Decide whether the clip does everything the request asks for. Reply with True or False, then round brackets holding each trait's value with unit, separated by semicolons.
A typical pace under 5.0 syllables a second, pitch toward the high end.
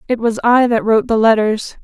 False (5.7 syllables/s; 230 Hz)